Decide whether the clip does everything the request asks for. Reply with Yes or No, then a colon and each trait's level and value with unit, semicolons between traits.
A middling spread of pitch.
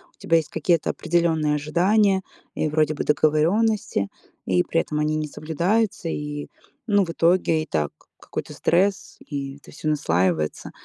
Yes: average, 3.0 semitones